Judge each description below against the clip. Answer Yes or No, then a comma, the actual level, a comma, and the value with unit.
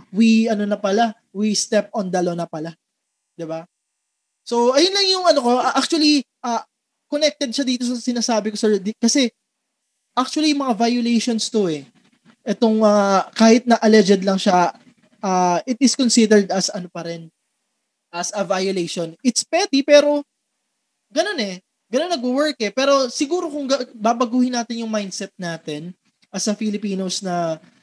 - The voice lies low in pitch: No, high, 225 Hz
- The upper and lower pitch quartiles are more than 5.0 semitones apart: No, average, 4.5 semitones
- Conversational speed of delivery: No, fast, 160 wpm